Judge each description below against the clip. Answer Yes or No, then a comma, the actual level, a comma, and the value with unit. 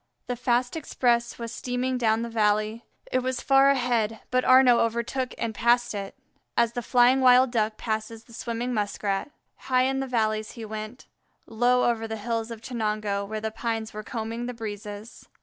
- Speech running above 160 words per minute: Yes, average, 180 wpm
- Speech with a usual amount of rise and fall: No, narrow, 2.3 semitones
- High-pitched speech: Yes, high, 235 Hz